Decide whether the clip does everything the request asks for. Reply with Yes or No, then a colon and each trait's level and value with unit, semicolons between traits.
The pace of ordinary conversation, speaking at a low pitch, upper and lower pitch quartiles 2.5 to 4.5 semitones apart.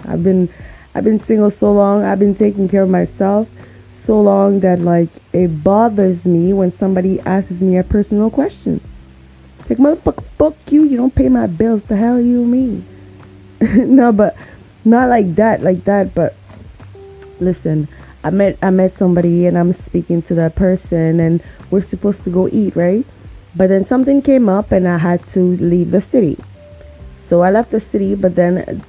No: average, 180 wpm; high, 190 Hz; average, 3.5 semitones